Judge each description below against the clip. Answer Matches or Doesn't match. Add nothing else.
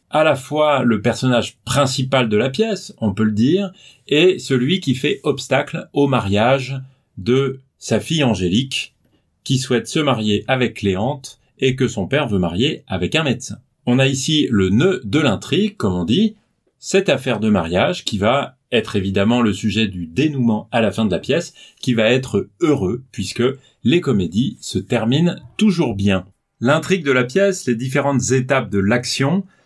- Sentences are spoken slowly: Doesn't match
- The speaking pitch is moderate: Doesn't match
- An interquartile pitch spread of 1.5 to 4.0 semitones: Doesn't match